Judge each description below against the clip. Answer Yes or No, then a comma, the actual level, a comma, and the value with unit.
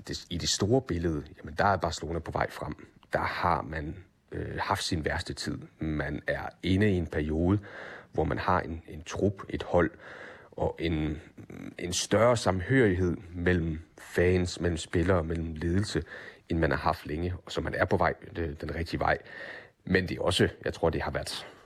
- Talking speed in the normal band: Yes, average, 190 wpm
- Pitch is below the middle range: Yes, very low, 85 Hz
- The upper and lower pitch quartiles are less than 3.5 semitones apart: Yes, narrow, 2.4 semitones